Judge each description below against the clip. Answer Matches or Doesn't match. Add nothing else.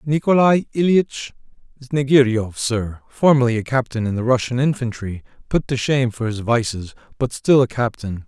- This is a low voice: Matches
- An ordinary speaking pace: Matches